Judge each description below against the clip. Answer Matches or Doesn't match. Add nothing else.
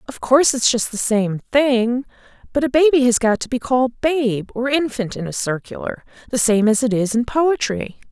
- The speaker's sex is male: Doesn't match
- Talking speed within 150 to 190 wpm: Doesn't match